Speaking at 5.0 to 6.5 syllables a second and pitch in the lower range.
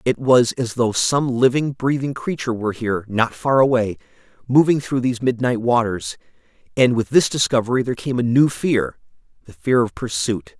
Yes: 5.3 syllables/s; low, 125 Hz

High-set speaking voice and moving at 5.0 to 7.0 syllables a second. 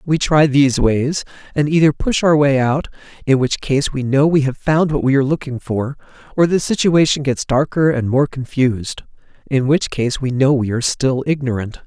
No: medium, 140 Hz; 5.1 syllables/s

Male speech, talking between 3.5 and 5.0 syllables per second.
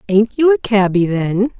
No: female; 4.5 syllables/s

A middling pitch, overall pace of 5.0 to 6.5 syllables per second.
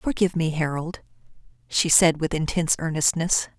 Yes: medium, 160 Hz; 5.4 syllables/s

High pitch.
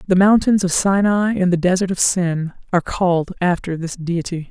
No: medium, 180 Hz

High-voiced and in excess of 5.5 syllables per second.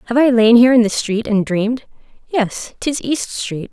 No: high, 230 Hz; 4.9 syllables/s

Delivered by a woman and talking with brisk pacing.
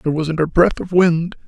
No: male; fast, 245 wpm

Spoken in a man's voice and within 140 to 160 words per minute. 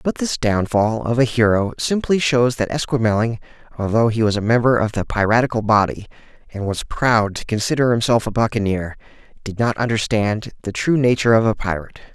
No: male; average, 180 wpm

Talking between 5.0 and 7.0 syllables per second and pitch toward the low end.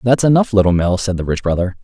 Yes: 6.5 syllables/s; low, 100 Hz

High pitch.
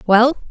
Yes: high, 245 Hz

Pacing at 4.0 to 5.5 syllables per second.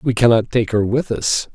Yes: 4.7 syllables/s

